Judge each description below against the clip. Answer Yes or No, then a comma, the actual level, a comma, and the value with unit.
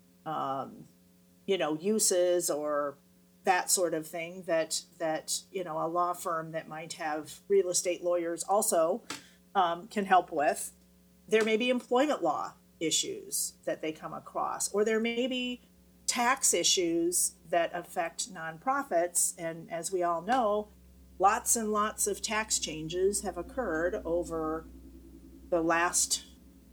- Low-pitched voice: No, medium, 175 Hz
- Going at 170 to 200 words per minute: No, average, 140 wpm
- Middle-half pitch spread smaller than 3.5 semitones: No, average, 5.1 semitones